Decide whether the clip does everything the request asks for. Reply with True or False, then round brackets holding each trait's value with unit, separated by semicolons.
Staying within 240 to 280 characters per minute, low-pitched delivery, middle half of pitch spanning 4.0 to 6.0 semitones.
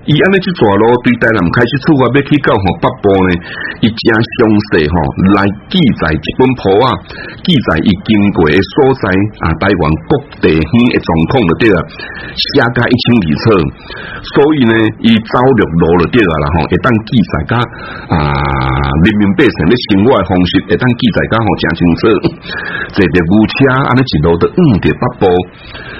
True (250 characters per minute; 105 Hz; 5.5 semitones)